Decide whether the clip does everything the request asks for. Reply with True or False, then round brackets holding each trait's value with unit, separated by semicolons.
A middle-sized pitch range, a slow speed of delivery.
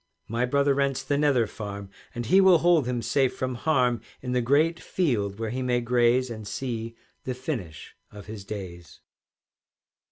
False (3.9 semitones; 170 wpm)